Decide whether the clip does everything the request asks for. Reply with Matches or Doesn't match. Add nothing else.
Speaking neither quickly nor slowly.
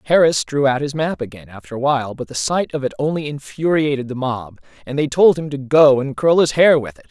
Doesn't match